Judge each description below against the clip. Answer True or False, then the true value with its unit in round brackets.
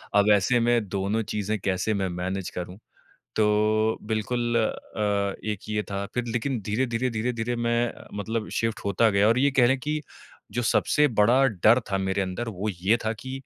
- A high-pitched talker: False (110 Hz)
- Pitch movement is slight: False (3.1 semitones)